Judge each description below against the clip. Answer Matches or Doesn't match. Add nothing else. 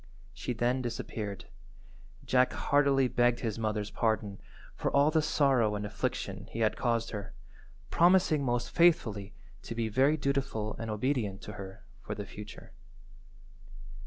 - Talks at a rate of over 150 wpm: Doesn't match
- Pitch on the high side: Doesn't match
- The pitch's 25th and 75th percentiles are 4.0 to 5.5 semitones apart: Matches